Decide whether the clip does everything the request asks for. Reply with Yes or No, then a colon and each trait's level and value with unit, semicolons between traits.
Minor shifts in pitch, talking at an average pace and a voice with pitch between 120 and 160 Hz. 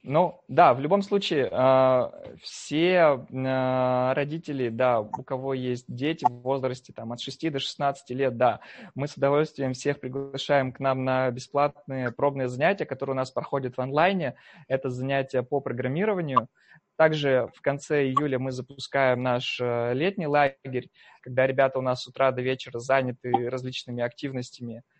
Yes: narrow, 1.9 semitones; average, 150 wpm; low, 130 Hz